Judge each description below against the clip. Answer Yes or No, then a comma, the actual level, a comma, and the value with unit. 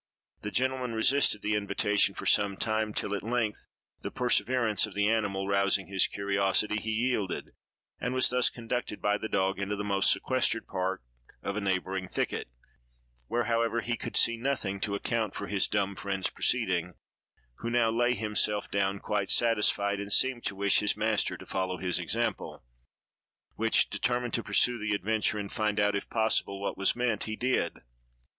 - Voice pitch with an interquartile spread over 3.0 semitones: No, average, 2.7 semitones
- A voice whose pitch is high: No, low, 105 Hz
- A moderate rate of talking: Yes, average, 175 wpm